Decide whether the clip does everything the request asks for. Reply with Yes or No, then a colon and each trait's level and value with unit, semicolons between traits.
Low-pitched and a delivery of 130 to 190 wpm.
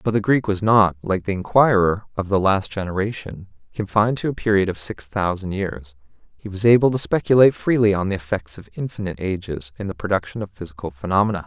No: low, 100 Hz; average, 200 wpm